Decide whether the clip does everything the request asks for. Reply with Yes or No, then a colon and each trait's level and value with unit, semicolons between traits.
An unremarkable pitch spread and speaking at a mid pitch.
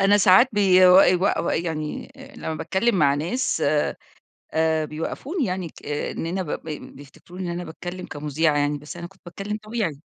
Yes: average, 3.8 semitones; medium, 175 Hz